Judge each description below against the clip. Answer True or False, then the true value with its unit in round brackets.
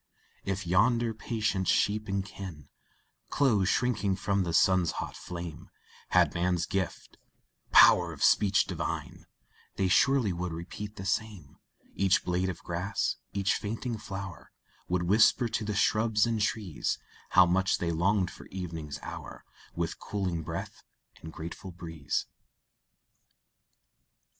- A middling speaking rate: False (130 wpm)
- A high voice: False (95 Hz)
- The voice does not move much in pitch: False (3.2 semitones)